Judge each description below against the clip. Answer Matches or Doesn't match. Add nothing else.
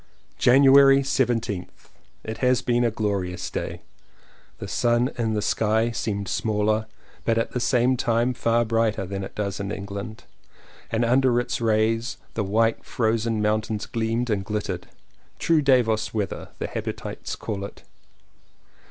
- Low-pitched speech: Matches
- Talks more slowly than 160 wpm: Matches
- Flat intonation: Matches